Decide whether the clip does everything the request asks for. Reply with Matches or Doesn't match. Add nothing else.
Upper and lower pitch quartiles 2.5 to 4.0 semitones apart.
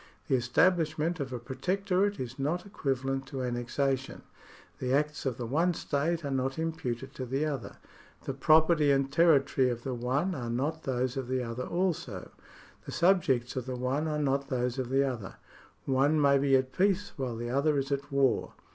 Matches